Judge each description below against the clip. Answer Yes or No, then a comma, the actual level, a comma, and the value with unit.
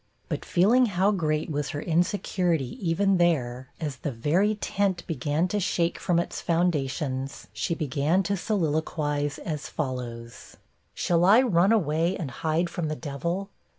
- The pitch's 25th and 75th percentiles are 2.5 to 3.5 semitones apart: No, average, 4.1 semitones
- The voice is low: No, medium, 165 Hz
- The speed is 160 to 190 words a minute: No, average, 150 wpm